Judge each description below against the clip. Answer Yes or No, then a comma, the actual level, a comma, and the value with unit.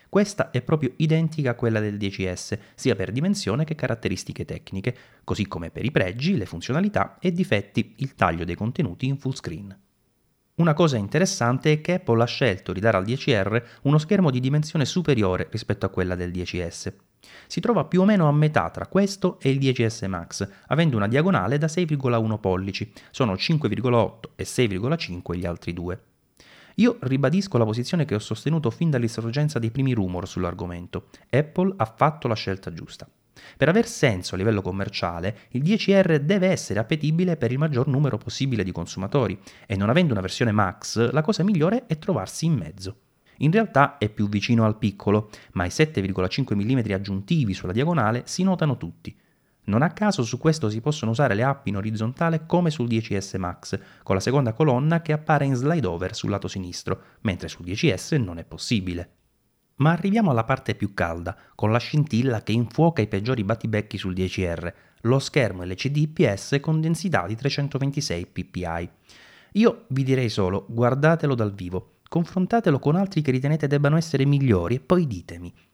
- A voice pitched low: Yes, low, 120 Hz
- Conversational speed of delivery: No, fast, 175 wpm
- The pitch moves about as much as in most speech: No, wide, 7.7 semitones